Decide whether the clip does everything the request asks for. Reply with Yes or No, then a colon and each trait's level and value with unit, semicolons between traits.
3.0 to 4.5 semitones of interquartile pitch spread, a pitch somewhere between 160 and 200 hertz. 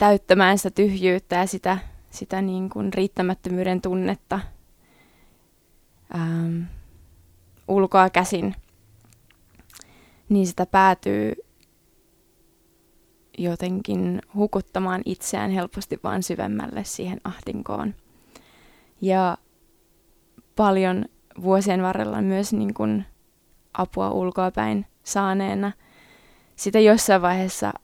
No: narrow, 2.5 semitones; medium, 185 Hz